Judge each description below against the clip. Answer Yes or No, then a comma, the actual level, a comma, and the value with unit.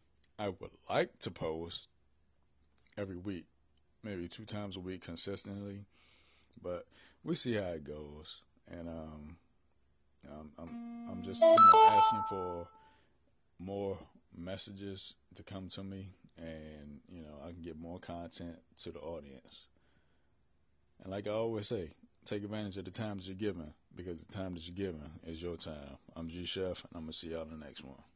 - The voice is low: Yes, very low, 85 Hz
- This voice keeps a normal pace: Yes, average, 170 wpm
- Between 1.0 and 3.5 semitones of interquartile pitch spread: No, average, 4.7 semitones